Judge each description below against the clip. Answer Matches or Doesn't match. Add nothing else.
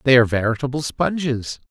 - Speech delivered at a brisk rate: Doesn't match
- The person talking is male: Matches